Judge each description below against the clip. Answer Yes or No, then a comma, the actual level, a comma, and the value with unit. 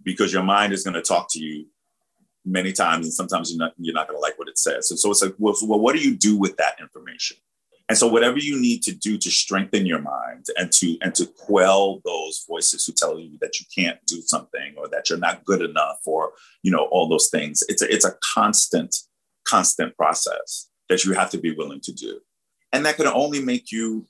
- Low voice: Yes, low, 125 Hz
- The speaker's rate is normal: No, fast, 235 wpm